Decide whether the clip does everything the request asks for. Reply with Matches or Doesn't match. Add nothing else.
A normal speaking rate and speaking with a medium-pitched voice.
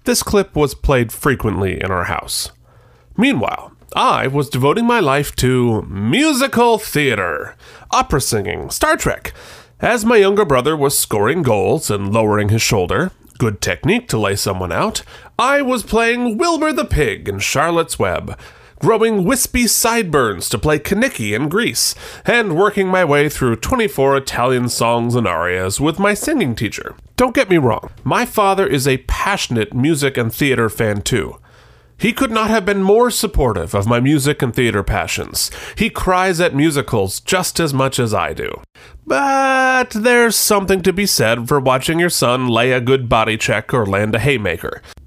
Matches